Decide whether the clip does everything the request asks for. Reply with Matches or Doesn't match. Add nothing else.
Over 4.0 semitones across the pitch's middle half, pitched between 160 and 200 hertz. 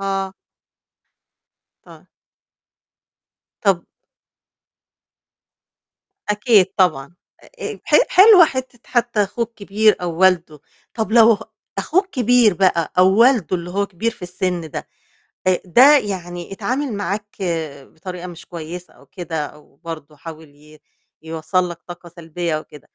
Matches